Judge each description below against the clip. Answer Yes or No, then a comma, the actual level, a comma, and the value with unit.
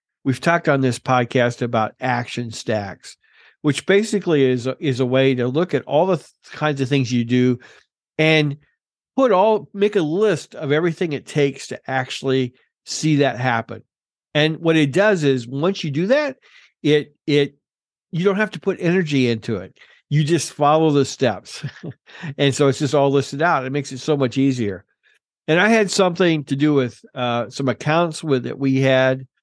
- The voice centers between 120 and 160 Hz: Yes, medium, 140 Hz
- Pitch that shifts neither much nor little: Yes, average, 3.9 semitones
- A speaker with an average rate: Yes, average, 190 wpm